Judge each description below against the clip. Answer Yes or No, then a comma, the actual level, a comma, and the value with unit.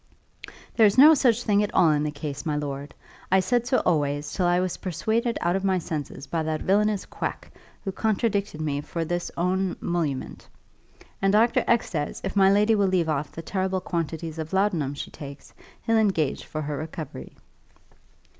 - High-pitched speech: No, medium, 175 Hz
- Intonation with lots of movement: No, average, 4.9 semitones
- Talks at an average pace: Yes, average, 185 wpm